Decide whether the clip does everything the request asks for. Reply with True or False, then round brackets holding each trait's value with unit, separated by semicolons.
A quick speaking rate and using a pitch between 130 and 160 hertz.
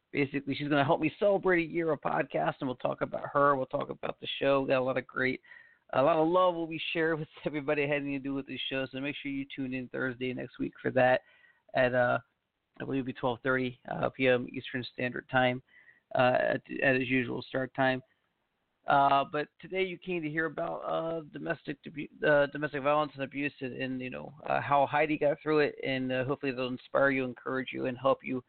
True (230 wpm; 140 Hz)